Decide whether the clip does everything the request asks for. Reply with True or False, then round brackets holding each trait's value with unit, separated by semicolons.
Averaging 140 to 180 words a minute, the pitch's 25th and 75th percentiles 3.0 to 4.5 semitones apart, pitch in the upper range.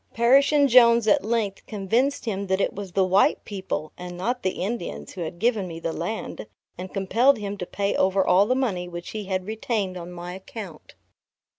False (200 wpm; 4.1 semitones; 195 Hz)